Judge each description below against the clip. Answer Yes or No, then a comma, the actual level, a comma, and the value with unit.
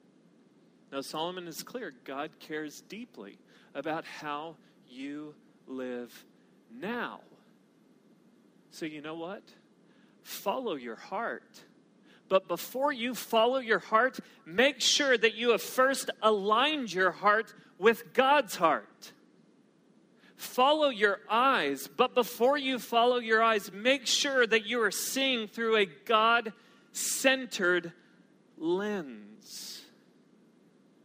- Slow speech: Yes, slow, 110 wpm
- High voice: Yes, high, 225 Hz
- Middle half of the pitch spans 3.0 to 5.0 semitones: No, wide, 5.6 semitones